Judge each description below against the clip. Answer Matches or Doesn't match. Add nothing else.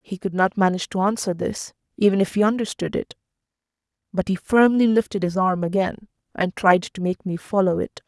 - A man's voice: Doesn't match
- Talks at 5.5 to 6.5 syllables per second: Matches